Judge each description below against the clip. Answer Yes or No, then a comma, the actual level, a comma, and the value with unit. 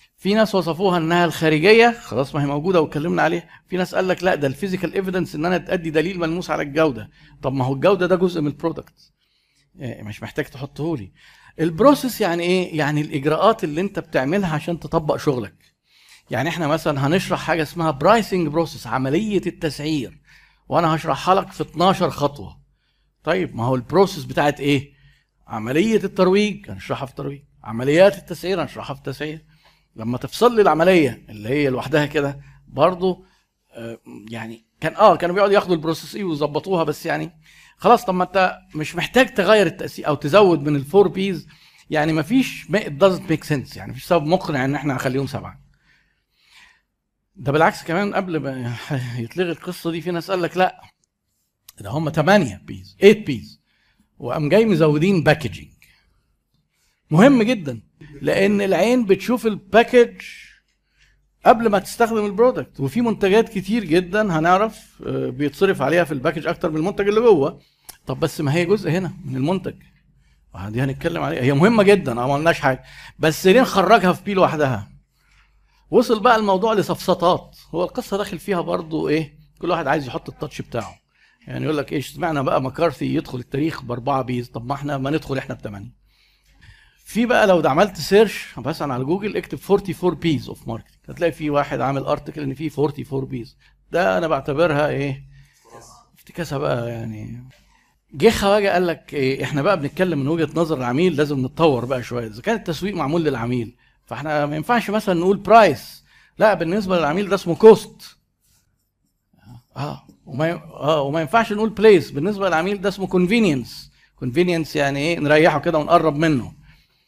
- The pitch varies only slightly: No, average, 5.1 semitones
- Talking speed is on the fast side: Yes, fast, 160 wpm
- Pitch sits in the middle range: Yes, medium, 160 Hz